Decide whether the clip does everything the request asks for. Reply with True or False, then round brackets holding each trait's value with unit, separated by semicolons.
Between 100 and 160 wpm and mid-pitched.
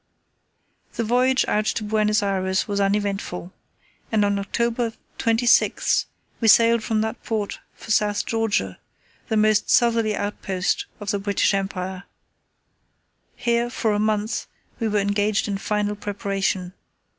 False (135 wpm; 210 Hz)